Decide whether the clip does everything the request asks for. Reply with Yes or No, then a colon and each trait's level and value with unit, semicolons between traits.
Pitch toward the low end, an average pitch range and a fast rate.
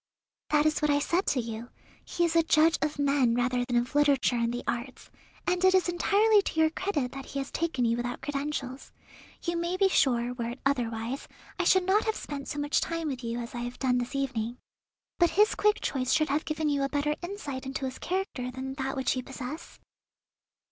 No: very high, 280 Hz; average, 4.9 semitones; fast, 220 wpm